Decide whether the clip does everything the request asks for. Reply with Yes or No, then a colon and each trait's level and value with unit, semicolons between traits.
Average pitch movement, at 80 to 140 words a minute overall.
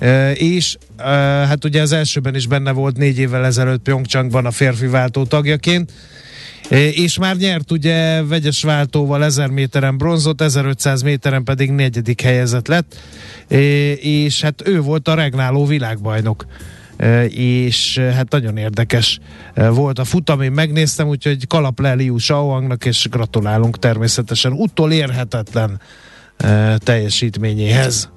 Yes: average, 3.6 semitones; average, 135 wpm